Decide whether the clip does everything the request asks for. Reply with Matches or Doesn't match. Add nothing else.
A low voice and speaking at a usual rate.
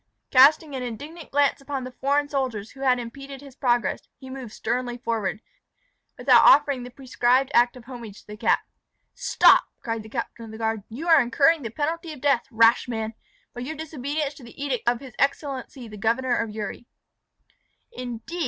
Doesn't match